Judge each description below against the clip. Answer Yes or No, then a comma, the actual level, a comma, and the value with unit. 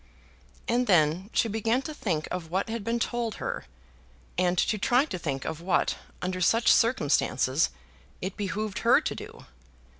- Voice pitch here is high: Yes, high, 195 Hz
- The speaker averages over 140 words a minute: Yes, average, 160 wpm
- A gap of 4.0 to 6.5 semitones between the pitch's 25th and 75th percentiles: Yes, average, 4.9 semitones